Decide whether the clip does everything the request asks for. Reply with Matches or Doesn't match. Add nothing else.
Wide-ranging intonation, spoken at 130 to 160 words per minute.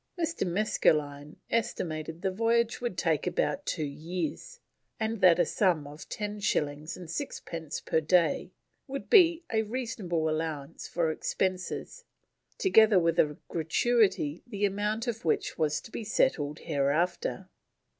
Matches